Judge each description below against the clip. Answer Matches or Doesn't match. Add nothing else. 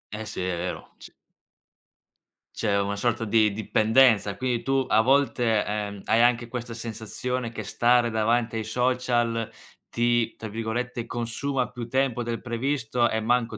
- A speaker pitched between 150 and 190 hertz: Doesn't match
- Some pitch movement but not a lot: Doesn't match